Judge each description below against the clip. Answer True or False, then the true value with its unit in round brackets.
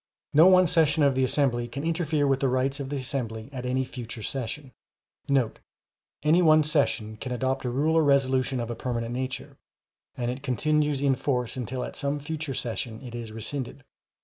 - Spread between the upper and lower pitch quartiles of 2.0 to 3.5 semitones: True (3.0 semitones)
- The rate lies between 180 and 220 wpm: True (185 wpm)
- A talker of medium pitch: False (130 Hz)